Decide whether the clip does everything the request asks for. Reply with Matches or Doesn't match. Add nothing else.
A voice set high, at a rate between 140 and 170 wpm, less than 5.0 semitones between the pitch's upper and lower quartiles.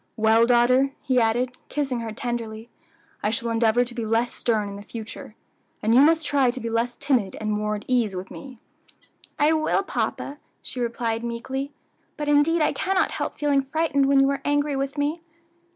Doesn't match